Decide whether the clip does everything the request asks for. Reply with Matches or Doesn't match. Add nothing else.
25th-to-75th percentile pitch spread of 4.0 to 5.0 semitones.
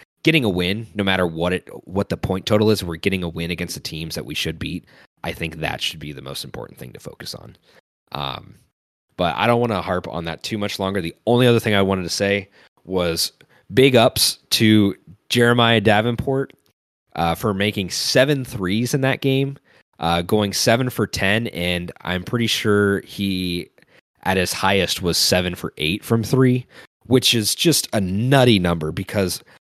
Matches